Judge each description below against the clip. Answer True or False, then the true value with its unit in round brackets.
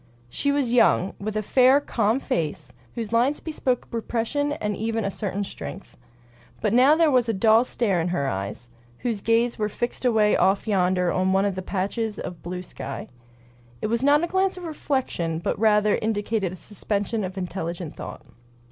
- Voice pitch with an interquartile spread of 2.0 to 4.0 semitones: False (4.6 semitones)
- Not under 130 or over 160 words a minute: False (185 wpm)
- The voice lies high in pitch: True (215 Hz)